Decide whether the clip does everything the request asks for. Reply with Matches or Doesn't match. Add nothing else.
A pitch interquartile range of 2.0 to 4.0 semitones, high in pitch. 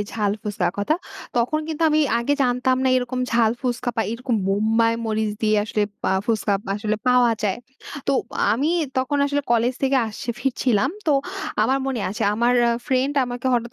Matches